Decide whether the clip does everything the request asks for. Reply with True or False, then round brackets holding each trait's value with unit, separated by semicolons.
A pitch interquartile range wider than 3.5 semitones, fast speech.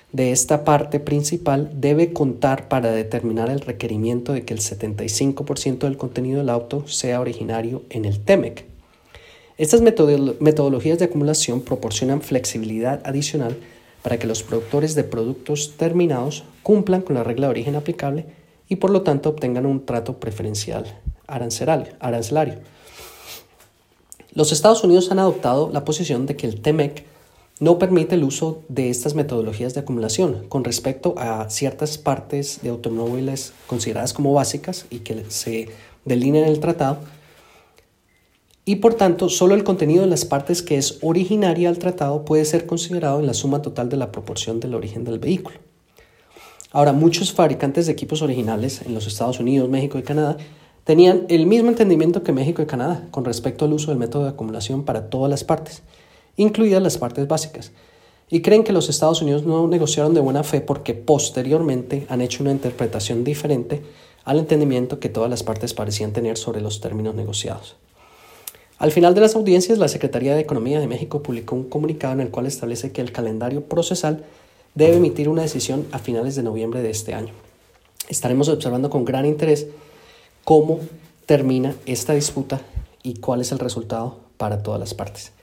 False (4.5 semitones; 165 wpm)